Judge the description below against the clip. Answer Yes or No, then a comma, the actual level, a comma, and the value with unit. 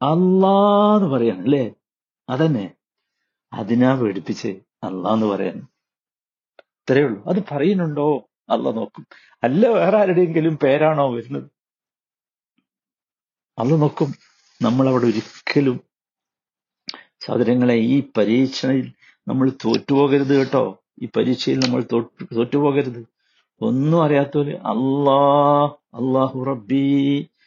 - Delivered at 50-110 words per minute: Yes, average, 85 wpm